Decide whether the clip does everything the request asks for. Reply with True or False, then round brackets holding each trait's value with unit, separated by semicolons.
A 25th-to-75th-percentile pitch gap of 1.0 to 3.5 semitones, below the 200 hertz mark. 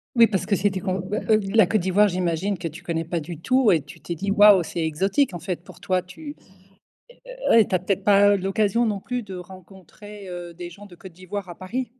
True (2.8 semitones; 190 Hz)